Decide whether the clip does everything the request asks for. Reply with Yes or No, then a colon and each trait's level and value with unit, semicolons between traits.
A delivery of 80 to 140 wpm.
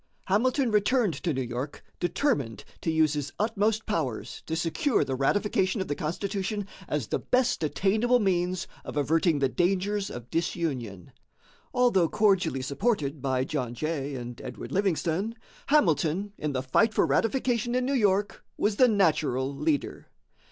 No: average, 150 wpm